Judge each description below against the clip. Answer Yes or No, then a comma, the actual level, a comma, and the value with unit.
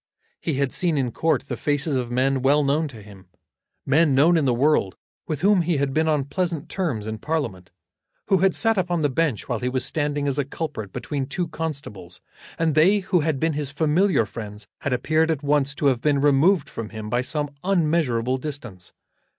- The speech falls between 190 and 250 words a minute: Yes, fast, 205 wpm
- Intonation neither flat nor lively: Yes, average, 4.1 semitones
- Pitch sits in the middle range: Yes, medium, 145 Hz